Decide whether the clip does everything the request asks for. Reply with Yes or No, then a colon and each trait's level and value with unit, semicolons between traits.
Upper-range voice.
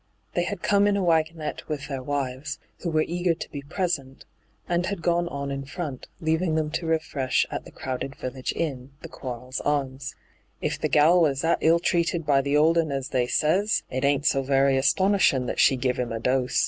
No: medium, 145 Hz